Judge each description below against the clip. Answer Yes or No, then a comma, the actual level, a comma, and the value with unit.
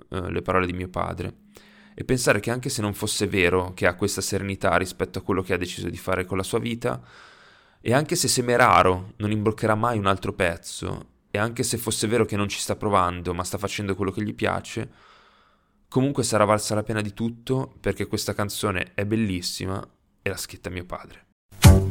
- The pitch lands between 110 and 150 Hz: No, low, 100 Hz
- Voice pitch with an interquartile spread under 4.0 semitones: Yes, average, 2.9 semitones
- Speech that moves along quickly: Yes, fast, 200 wpm